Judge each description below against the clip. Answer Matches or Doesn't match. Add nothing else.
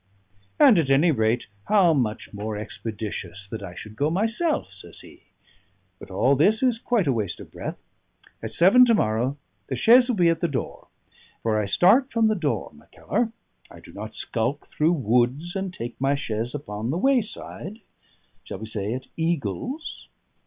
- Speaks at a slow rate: Doesn't match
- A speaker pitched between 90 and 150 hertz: Matches